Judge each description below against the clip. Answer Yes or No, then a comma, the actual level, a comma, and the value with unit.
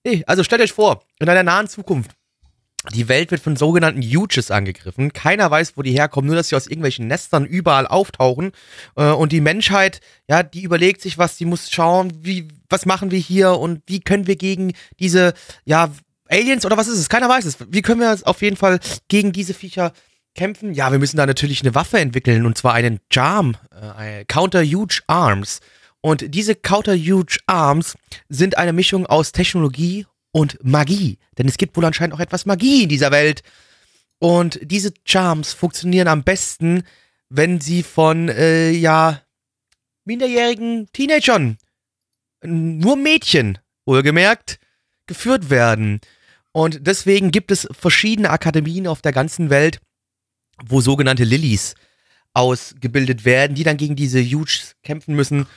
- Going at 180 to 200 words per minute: No, average, 160 wpm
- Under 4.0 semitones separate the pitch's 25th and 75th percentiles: No, wide, 5.4 semitones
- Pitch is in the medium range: Yes, medium, 165 Hz